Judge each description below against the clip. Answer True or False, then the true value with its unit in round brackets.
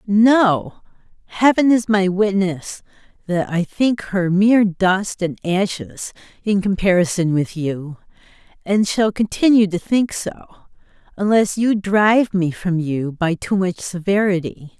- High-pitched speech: True (195 Hz)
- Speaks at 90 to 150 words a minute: True (135 wpm)